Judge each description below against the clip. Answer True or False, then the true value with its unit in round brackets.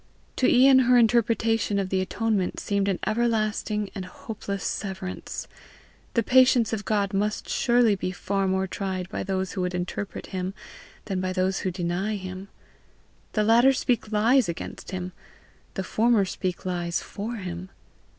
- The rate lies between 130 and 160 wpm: True (155 wpm)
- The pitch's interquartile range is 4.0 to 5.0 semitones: False (3.3 semitones)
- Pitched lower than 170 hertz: False (200 Hz)